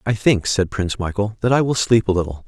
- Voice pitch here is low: Yes, low, 105 Hz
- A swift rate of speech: Yes, fast, 265 wpm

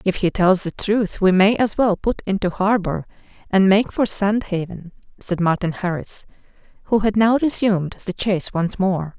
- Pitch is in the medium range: No, high, 195 Hz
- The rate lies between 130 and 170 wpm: No, average, 185 wpm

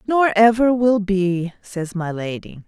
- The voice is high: Yes, high, 200 Hz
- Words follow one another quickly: No, average, 155 wpm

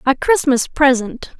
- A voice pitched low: No, very high, 270 Hz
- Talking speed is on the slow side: Yes, slow, 130 wpm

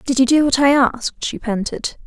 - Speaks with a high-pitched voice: Yes, very high, 260 Hz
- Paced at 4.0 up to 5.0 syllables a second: No, 5.2 syllables/s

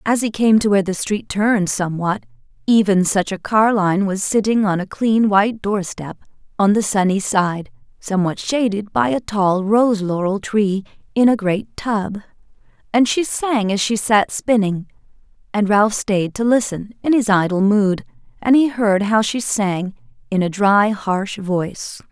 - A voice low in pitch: No, high, 200 Hz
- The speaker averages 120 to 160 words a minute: No, average, 175 wpm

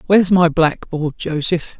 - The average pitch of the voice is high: No, medium, 165 Hz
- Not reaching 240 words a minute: Yes, slow, 135 wpm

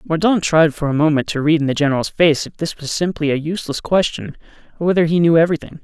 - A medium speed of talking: No, fast, 235 wpm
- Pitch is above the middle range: No, medium, 160 Hz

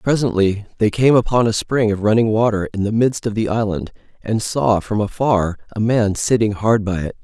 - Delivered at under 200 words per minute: No, fast, 205 wpm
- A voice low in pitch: Yes, low, 110 Hz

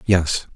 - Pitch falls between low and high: No, very low, 85 Hz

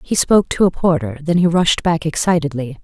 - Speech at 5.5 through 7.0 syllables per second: Yes, 5.6 syllables/s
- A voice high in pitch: No, medium, 160 Hz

